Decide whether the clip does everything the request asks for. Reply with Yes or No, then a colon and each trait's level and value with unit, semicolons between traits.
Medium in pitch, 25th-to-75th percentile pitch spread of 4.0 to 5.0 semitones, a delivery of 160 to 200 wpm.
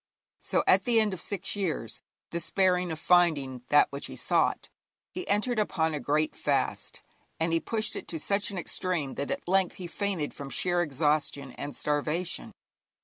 Yes: medium, 170 Hz; average, 4.5 semitones; average, 175 wpm